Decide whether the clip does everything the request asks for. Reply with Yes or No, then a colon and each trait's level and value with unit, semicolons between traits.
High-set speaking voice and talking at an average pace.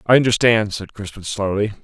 No: low, 110 Hz; average, 165 wpm